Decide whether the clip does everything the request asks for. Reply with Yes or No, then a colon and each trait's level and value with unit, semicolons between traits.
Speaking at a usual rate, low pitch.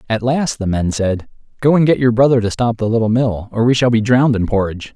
No: fast, 265 wpm; low, 115 Hz